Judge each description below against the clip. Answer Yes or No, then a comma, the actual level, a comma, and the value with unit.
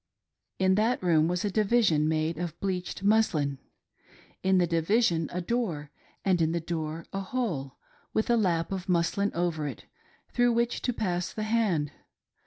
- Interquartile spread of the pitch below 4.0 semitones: No, average, 4.7 semitones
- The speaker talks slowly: No, average, 165 wpm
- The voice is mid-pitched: Yes, medium, 180 Hz